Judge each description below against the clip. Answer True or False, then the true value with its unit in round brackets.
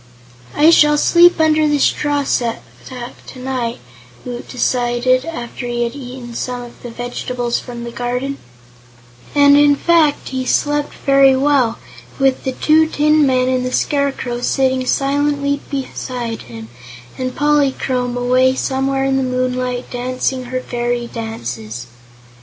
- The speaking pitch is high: True (255 Hz)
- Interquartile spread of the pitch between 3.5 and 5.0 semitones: False (2.7 semitones)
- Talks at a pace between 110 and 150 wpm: True (135 wpm)